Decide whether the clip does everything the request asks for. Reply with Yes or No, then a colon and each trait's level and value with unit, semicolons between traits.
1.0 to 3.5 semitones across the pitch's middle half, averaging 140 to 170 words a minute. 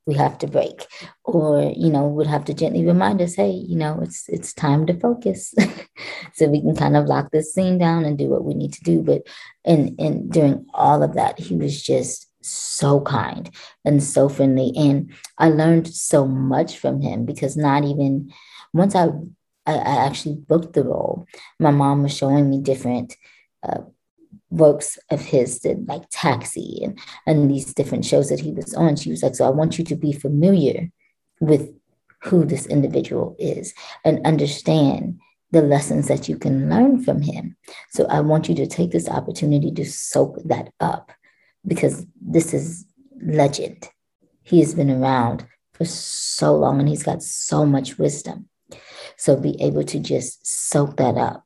No: average, 2.9 semitones; average, 180 wpm